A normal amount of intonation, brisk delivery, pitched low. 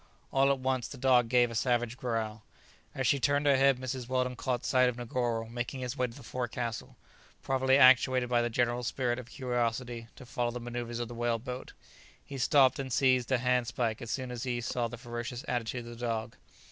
No: narrow, 1.5 semitones; fast, 210 wpm; low, 125 Hz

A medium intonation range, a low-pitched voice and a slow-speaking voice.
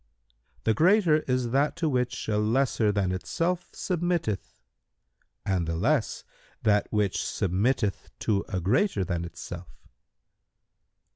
No: wide, 7.4 semitones; low, 110 Hz; slow, 125 wpm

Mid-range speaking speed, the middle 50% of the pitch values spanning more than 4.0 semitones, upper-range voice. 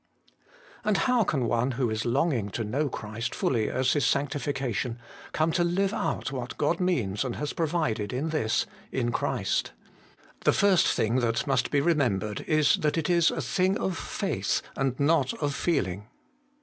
No: average, 175 wpm; wide, 5.4 semitones; low, 135 Hz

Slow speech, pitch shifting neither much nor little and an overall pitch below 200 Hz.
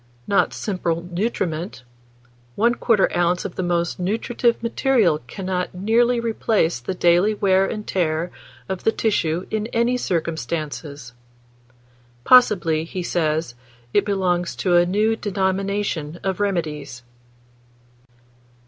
Yes: slow, 110 wpm; average, 4.0 semitones; medium, 185 Hz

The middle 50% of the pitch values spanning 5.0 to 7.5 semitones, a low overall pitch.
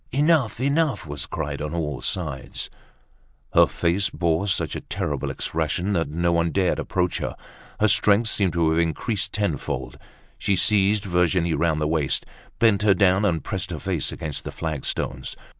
No: average, 4.2 semitones; very low, 90 Hz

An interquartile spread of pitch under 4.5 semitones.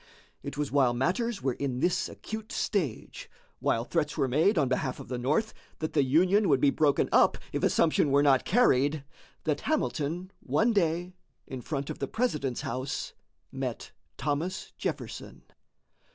No: average, 5.1 semitones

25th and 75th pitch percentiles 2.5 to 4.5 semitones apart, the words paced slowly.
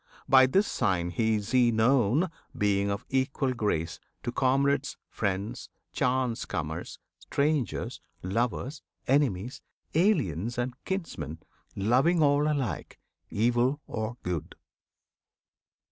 No: wide, 5.4 semitones; slow, 100 wpm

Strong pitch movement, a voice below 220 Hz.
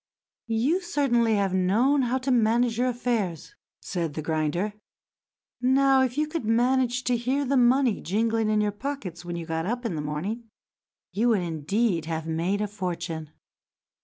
No: wide, 6.2 semitones; high, 225 Hz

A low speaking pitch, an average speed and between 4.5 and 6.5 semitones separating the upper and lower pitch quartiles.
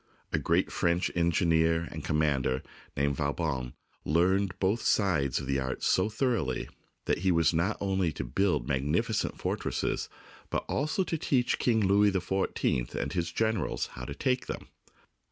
Yes: very low, 85 Hz; average, 160 wpm; wide, 5.6 semitones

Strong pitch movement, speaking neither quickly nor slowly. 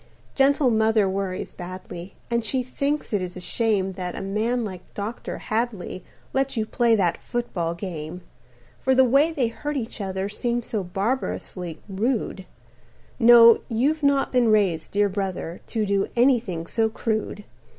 No: average, 4.2 semitones; average, 155 wpm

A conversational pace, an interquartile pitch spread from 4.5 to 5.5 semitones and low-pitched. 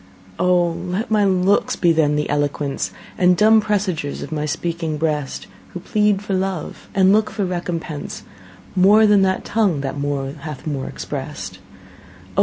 No: average, 160 wpm; average, 4.8 semitones; medium, 180 Hz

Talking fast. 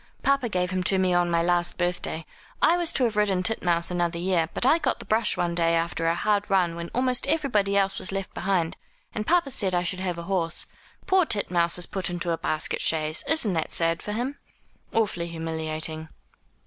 Yes: fast, 210 wpm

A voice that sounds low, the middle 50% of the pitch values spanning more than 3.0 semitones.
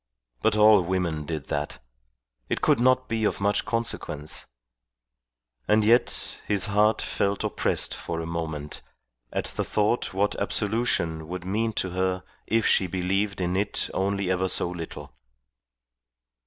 Yes: very low, 95 Hz; average, 3.5 semitones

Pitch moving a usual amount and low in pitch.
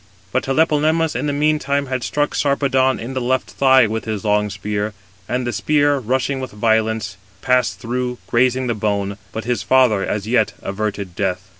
Yes: average, 4.1 semitones; low, 125 Hz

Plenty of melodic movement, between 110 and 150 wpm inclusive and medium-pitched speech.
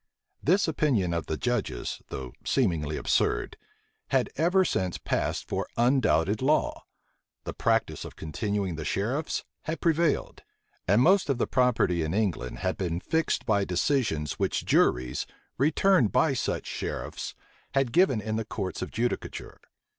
No: wide, 8.1 semitones; average, 145 wpm; low, 110 Hz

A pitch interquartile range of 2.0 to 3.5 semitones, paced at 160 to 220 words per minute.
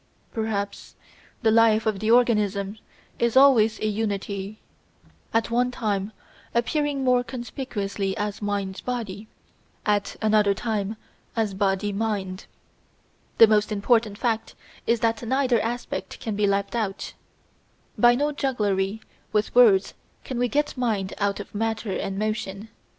No: average, 2.8 semitones; slow, 135 wpm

